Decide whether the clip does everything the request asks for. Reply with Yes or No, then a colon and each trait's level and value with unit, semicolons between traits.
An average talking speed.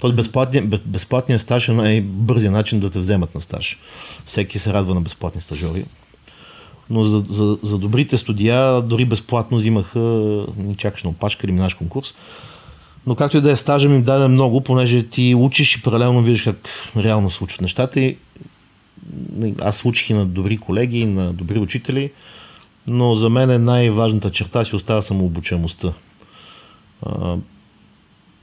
Yes: average, 155 wpm